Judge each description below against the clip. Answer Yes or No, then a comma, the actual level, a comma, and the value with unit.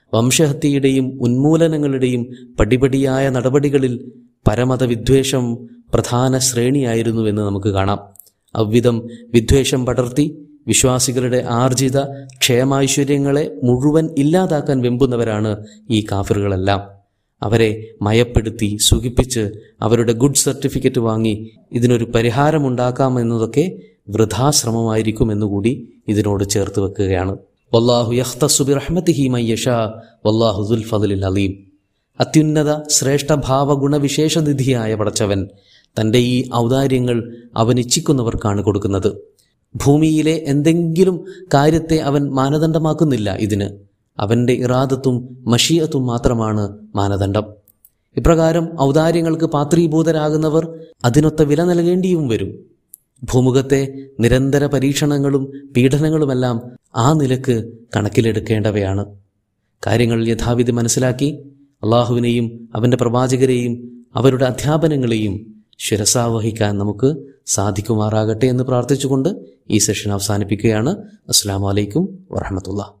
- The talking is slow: No, average, 75 wpm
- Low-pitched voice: Yes, low, 125 Hz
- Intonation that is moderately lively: Yes, average, 4.3 semitones